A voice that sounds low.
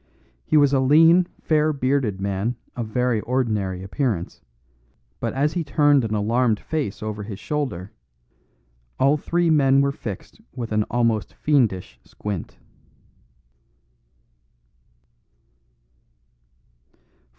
Yes: low, 125 Hz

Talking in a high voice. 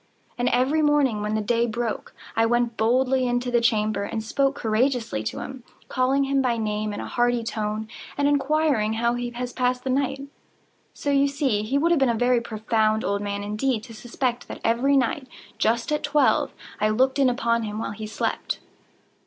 Yes: high, 240 Hz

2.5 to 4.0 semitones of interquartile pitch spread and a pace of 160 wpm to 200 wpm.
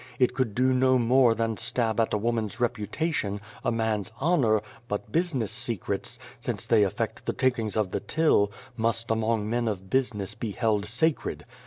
Yes: average, 3.0 semitones; average, 170 wpm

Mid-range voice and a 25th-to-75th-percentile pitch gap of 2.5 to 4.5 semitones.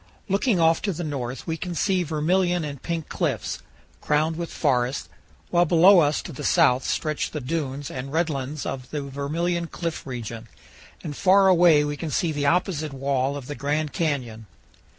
Yes: medium, 150 Hz; average, 3.7 semitones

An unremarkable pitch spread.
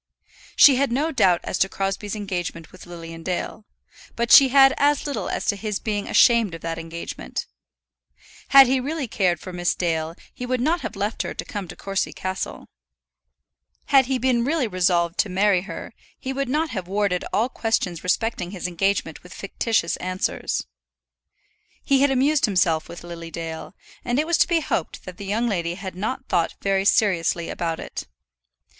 No: wide, 6.3 semitones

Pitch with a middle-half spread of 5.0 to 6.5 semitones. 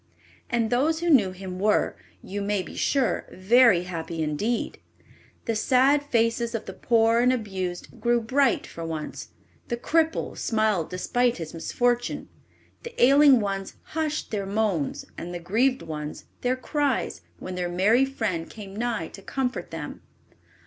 Yes: wide, 5.4 semitones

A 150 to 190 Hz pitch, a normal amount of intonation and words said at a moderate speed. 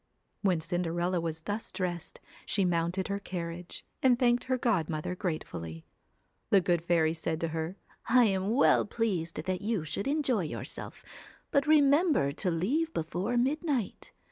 No: medium, 185 Hz; wide, 6.4 semitones; average, 155 wpm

